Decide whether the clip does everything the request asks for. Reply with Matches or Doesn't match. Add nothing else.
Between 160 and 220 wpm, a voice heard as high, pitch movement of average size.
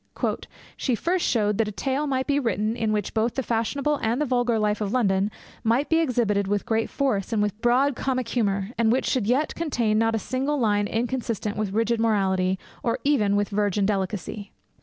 Matches